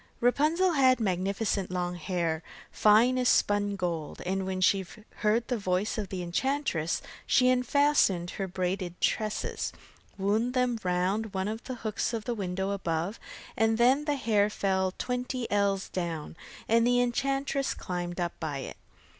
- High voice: Yes, high, 205 Hz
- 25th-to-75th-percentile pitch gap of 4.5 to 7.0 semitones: Yes, average, 5.2 semitones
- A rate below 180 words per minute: Yes, average, 155 wpm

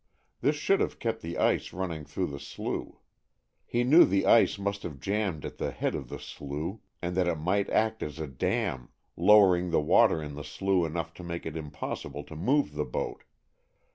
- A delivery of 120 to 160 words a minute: No, average, 200 wpm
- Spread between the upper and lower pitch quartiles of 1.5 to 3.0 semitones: No, average, 5.0 semitones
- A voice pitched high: No, very low, 85 Hz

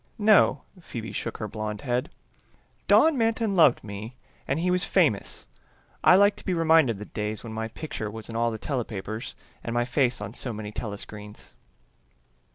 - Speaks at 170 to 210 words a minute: Yes, average, 175 wpm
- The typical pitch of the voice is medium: No, low, 115 Hz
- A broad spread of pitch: Yes, wide, 7.2 semitones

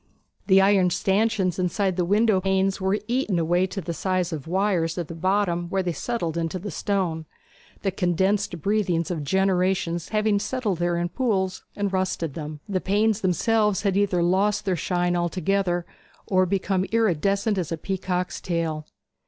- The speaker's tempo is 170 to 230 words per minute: No, average, 160 wpm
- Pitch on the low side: No, medium, 185 Hz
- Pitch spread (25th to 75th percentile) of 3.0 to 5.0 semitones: No, narrow, 2.5 semitones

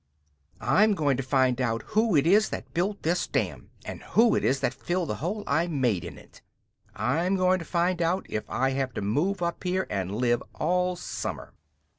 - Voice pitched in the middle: Yes, medium, 170 Hz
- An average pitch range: No, wide, 6.0 semitones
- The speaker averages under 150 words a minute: No, average, 200 wpm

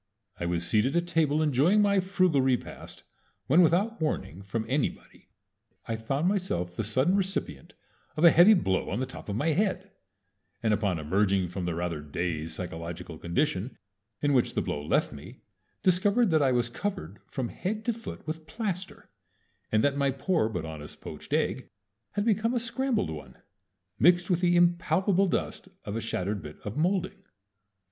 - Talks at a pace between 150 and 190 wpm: Yes, average, 170 wpm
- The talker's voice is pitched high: No, medium, 140 Hz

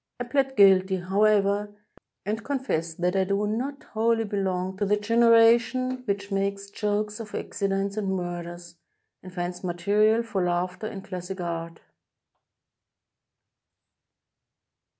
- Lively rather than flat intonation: No, average, 3.0 semitones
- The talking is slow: Yes, slow, 115 wpm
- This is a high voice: Yes, high, 200 Hz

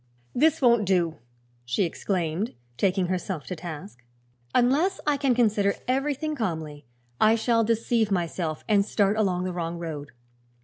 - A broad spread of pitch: Yes, wide, 5.8 semitones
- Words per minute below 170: Yes, average, 140 wpm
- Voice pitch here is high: Yes, high, 200 Hz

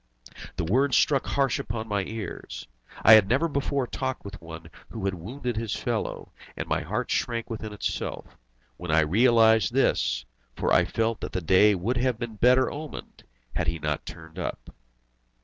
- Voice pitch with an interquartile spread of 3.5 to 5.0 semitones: No, wide, 5.6 semitones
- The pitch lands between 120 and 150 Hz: No, low, 110 Hz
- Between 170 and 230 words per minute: Yes, average, 175 wpm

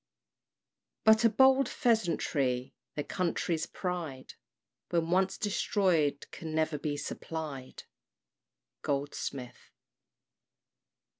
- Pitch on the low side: No, medium, 165 Hz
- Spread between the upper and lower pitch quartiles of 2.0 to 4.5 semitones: No, average, 5.1 semitones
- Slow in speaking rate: Yes, slow, 80 wpm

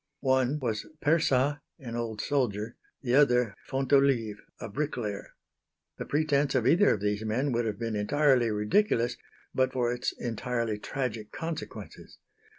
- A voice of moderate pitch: No, low, 125 Hz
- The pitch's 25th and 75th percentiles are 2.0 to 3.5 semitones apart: No, average, 4.0 semitones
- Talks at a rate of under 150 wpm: Yes, average, 140 wpm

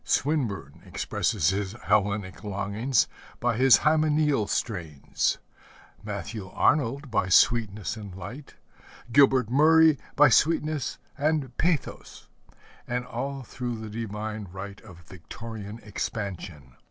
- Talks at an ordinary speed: No, slow, 105 wpm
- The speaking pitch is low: Yes, low, 110 Hz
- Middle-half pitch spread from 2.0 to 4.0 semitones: No, average, 5.1 semitones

